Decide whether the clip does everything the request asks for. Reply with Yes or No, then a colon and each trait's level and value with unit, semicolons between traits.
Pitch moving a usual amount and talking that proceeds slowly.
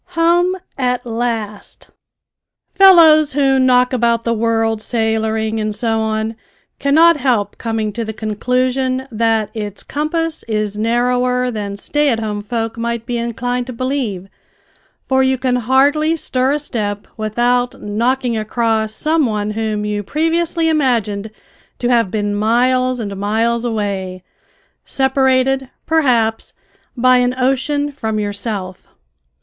Yes: average, 3.3 semitones; slow, 130 wpm